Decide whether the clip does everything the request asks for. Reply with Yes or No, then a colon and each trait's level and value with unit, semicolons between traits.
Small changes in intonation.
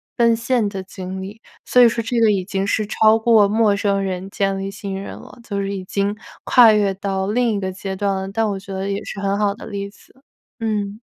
Yes: narrow, 1.9 semitones